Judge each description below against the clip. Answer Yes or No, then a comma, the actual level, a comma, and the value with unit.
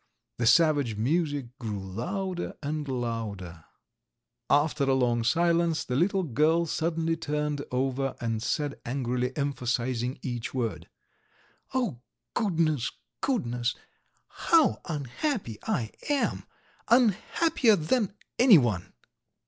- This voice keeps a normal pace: No, slow, 100 wpm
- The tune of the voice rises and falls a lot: Yes, wide, 6.0 semitones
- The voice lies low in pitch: No, medium, 145 Hz